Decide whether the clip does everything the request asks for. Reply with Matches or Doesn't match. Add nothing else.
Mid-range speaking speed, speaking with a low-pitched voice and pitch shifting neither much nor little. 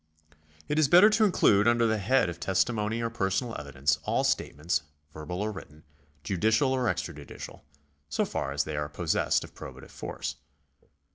Doesn't match